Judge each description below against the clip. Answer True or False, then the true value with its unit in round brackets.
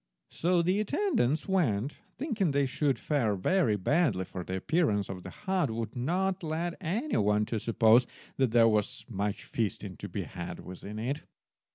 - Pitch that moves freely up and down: True (8.7 semitones)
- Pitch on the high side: False (135 Hz)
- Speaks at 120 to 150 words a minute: False (175 wpm)